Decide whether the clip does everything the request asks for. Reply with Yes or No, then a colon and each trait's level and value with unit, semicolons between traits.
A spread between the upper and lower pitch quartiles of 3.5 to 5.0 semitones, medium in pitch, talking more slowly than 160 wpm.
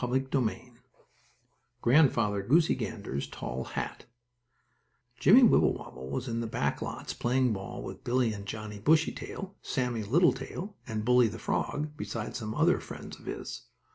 No: average, 3.9 semitones; low, 120 Hz; average, 140 wpm